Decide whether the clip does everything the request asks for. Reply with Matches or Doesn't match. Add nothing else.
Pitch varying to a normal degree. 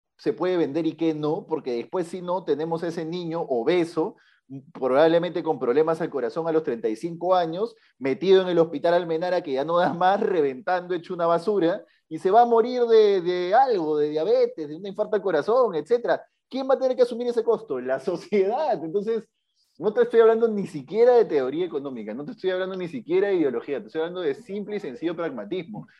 Doesn't match